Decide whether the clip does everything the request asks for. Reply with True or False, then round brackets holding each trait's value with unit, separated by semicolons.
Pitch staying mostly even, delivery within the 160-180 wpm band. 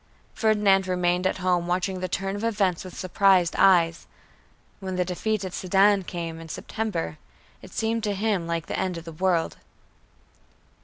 True (2.3 semitones; 165 wpm)